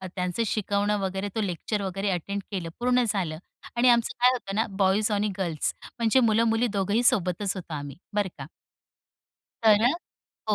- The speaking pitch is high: Yes, high, 205 Hz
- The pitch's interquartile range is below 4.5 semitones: Yes, average, 3.0 semitones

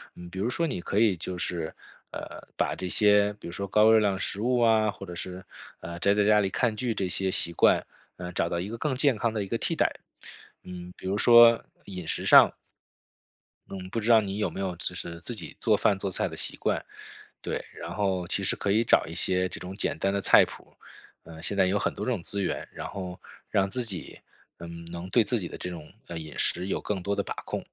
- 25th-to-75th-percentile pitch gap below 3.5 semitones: Yes, average, 2.9 semitones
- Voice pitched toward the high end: No, very low, 95 Hz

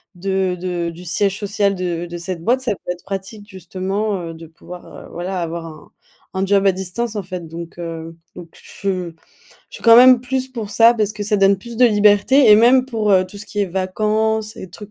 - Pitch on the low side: No, high, 195 Hz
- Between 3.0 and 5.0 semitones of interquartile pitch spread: Yes, average, 3.3 semitones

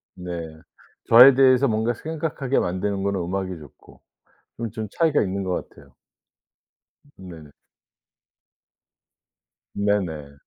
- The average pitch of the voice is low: Yes, low, 100 Hz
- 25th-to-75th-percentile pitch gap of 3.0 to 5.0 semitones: No, wide, 5.6 semitones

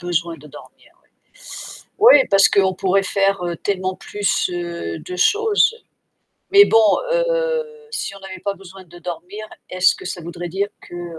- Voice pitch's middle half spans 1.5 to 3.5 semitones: Yes, average, 3.0 semitones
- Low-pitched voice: No, high, 190 Hz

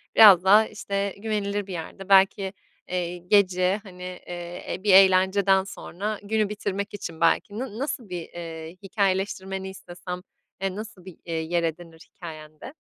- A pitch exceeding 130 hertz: Yes, high, 190 Hz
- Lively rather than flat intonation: No, narrow, 2.4 semitones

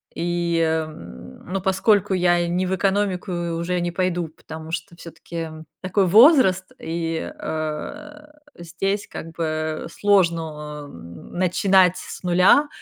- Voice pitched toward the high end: No, medium, 175 Hz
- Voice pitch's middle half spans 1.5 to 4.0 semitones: Yes, average, 2.9 semitones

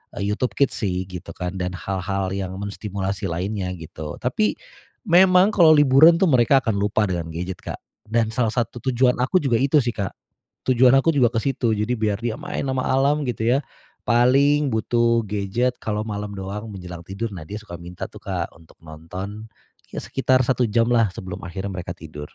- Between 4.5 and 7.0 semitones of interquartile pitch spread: Yes, average, 5.2 semitones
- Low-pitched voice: Yes, low, 110 Hz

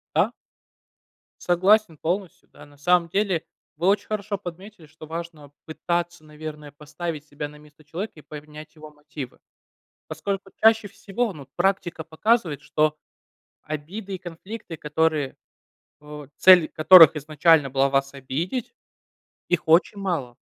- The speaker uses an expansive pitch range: No, average, 3.9 semitones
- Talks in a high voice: No, medium, 160 Hz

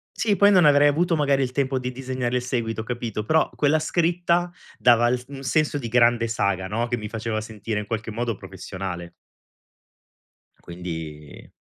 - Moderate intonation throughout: Yes, average, 4.9 semitones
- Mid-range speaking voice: No, low, 120 Hz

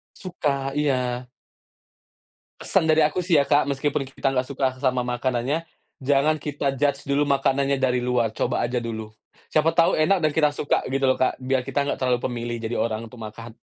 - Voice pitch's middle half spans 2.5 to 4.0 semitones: Yes, average, 2.8 semitones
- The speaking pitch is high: No, low, 135 Hz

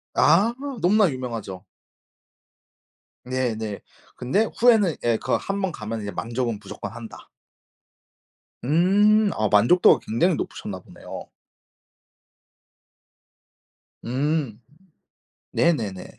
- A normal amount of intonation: No, wide, 9.0 semitones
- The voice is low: Yes, low, 130 Hz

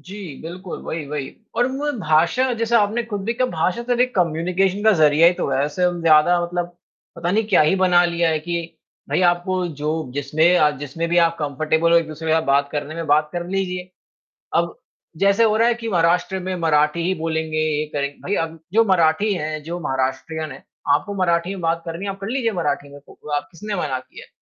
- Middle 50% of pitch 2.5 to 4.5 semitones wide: Yes, average, 3.4 semitones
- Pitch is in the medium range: Yes, medium, 170 Hz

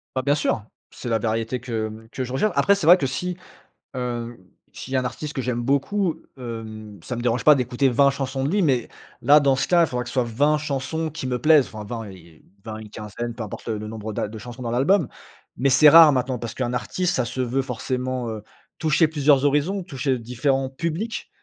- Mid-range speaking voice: No, low, 130 Hz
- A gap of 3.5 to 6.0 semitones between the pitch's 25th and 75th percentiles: Yes, average, 3.8 semitones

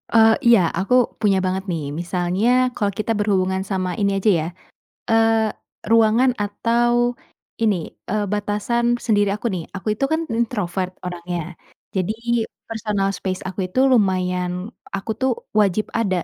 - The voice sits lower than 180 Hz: No, high, 205 Hz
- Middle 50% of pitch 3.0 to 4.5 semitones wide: Yes, average, 3.3 semitones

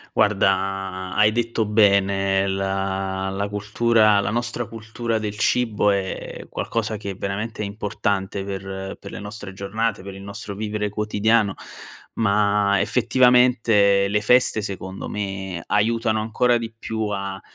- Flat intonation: Yes, narrow, 2.2 semitones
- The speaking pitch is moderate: No, low, 105 Hz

